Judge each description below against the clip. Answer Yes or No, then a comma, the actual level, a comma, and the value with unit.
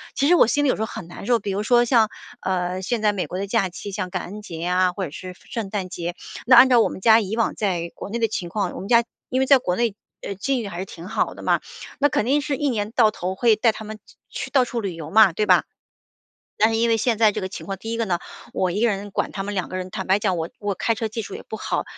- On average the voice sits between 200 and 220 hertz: Yes, high, 210 Hz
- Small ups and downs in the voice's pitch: No, average, 3.7 semitones